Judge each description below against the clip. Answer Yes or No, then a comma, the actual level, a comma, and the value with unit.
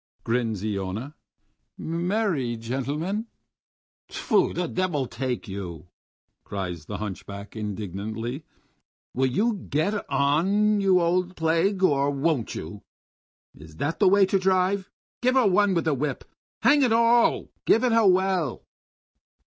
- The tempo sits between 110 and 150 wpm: Yes, average, 140 wpm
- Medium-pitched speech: Yes, medium, 155 Hz